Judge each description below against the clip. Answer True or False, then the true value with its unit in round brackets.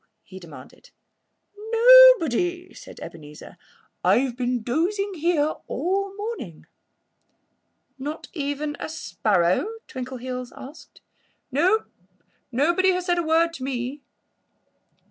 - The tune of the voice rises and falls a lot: True (6.4 semitones)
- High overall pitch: True (295 Hz)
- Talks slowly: True (105 wpm)